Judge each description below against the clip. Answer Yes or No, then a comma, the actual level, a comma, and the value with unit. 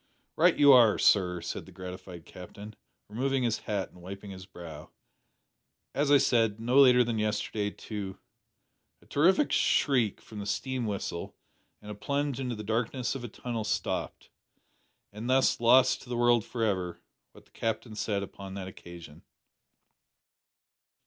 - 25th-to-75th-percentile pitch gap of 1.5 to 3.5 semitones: No, average, 4.2 semitones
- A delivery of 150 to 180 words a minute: Yes, average, 160 wpm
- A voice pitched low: Yes, low, 110 Hz